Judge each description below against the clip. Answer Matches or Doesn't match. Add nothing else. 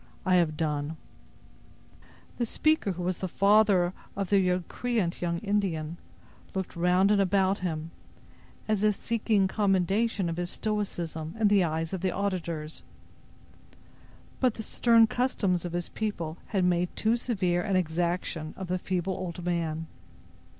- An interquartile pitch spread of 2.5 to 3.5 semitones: Matches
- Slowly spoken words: Doesn't match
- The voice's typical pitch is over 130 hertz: Matches